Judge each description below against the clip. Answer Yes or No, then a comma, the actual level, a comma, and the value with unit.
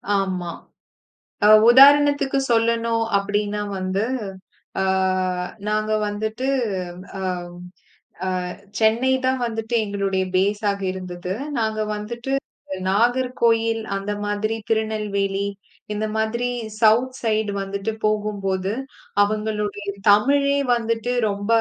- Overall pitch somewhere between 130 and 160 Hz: No, high, 215 Hz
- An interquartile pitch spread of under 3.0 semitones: Yes, narrow, 2.4 semitones